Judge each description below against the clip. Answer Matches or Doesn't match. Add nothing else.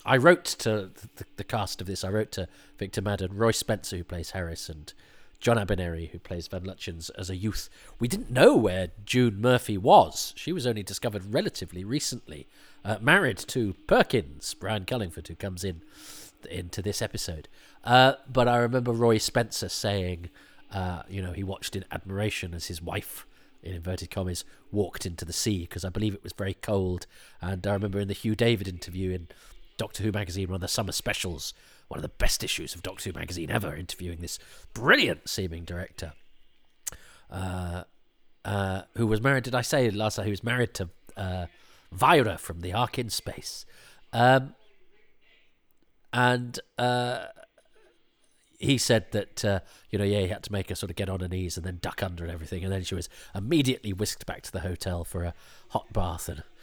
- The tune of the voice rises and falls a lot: Doesn't match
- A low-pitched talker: Matches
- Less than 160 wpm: Doesn't match